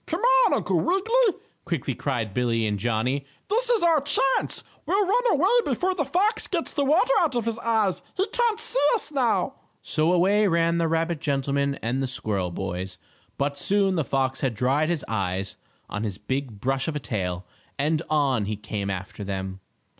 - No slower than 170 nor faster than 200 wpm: Yes, average, 185 wpm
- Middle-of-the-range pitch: Yes, medium, 150 Hz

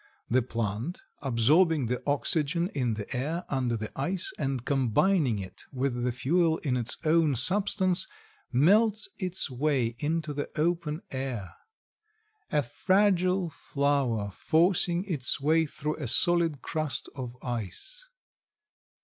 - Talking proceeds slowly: Yes, slow, 125 wpm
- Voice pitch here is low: No, medium, 145 Hz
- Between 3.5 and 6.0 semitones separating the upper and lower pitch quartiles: Yes, wide, 5.5 semitones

